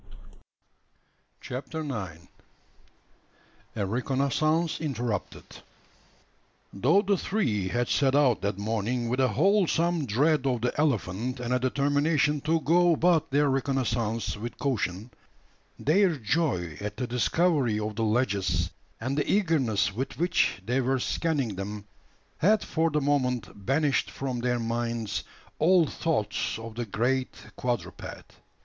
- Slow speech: Yes, slow, 130 wpm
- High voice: No, low, 130 Hz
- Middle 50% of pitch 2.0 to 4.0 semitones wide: No, average, 5.3 semitones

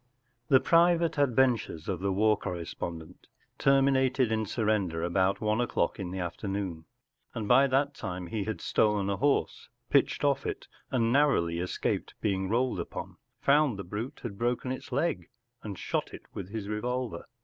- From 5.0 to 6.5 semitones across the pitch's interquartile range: Yes, wide, 5.5 semitones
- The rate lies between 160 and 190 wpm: Yes, average, 170 wpm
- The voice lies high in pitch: No, low, 110 Hz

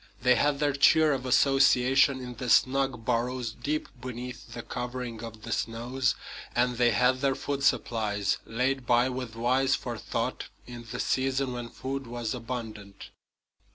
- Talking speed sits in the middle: Yes, average, 155 wpm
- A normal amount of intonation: No, narrow, 2.1 semitones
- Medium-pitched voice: No, low, 125 Hz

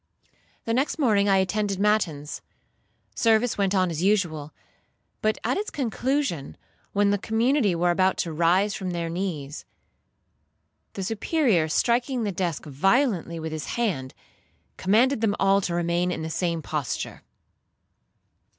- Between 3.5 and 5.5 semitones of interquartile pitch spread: Yes, average, 4.8 semitones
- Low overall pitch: No, high, 195 Hz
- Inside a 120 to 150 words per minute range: Yes, average, 140 wpm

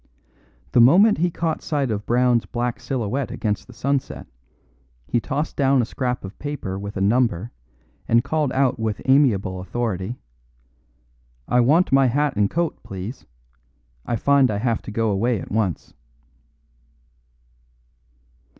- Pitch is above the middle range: No, low, 120 Hz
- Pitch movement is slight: No, average, 4.5 semitones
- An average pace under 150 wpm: Yes, average, 140 wpm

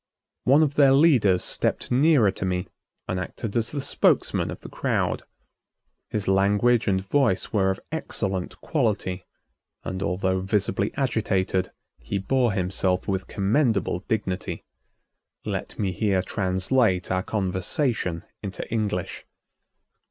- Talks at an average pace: No, slow, 125 wpm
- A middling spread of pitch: Yes, average, 4.2 semitones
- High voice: No, low, 100 Hz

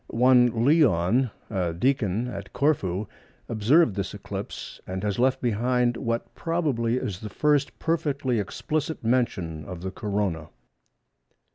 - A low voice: Yes, low, 115 Hz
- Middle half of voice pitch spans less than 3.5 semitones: No, average, 5.0 semitones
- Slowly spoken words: Yes, slow, 125 wpm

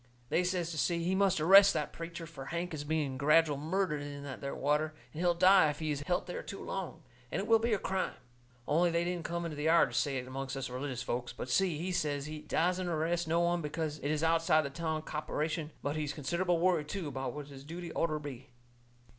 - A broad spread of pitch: No, average, 3.1 semitones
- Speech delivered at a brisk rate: Yes, fast, 235 wpm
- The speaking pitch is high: No, medium, 155 Hz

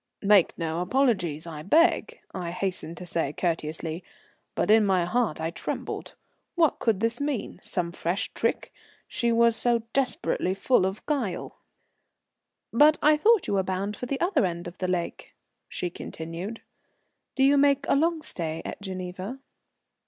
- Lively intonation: Yes, wide, 7.0 semitones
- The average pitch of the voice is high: Yes, high, 195 Hz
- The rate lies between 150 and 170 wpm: Yes, average, 160 wpm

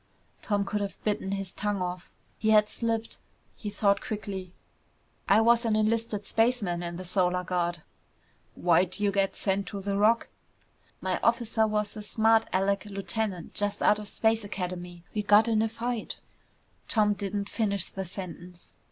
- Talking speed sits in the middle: Yes, average, 165 wpm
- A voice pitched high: Yes, high, 205 Hz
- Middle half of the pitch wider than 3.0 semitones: No, narrow, 2.6 semitones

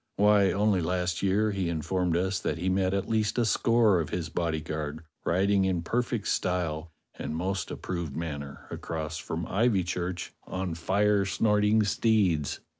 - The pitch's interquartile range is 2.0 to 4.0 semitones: Yes, average, 3.6 semitones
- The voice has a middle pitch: No, very low, 95 Hz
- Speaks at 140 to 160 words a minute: Yes, average, 155 wpm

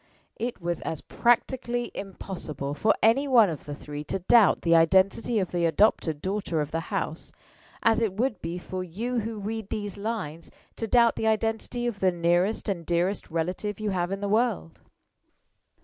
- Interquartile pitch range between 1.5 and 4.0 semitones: No, average, 4.7 semitones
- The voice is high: Yes, high, 195 Hz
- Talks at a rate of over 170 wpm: Yes, average, 180 wpm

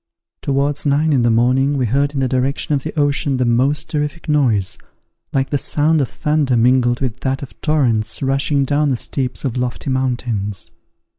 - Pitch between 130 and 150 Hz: Yes, low, 135 Hz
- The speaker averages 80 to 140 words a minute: No, average, 180 wpm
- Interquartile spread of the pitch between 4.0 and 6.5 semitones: No, narrow, 2.6 semitones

